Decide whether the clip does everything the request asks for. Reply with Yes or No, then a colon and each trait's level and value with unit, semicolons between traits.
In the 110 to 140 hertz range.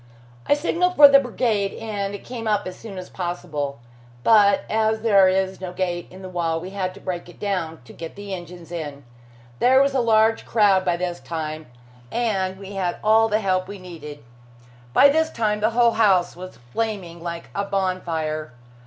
No: high, 190 Hz